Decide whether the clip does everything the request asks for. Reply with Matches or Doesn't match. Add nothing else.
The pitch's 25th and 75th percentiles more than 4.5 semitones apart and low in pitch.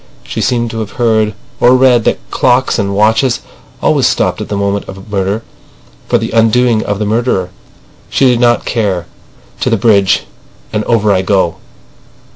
Doesn't match